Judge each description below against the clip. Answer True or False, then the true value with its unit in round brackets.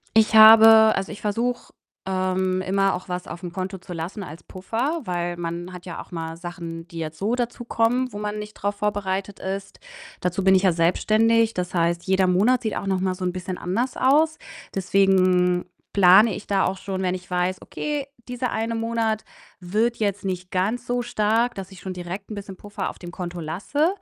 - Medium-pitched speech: False (195 Hz)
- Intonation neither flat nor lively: True (3.5 semitones)